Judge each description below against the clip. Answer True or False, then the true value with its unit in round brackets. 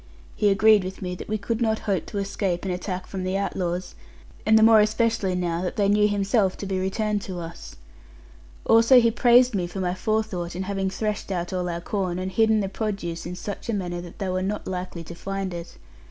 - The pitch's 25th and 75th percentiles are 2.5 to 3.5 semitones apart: True (2.8 semitones)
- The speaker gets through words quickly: True (225 wpm)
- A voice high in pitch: True (195 Hz)